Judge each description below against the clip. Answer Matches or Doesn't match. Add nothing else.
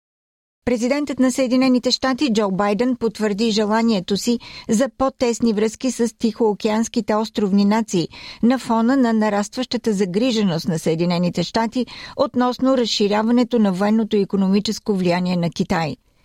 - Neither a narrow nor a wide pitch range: Matches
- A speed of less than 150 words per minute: Matches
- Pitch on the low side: Doesn't match